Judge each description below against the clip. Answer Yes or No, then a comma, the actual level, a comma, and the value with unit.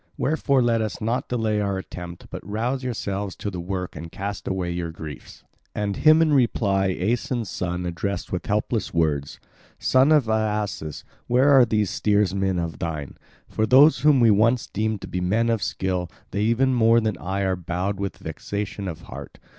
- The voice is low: Yes, low, 100 Hz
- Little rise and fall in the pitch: No, average, 4.3 semitones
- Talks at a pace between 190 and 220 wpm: No, average, 180 wpm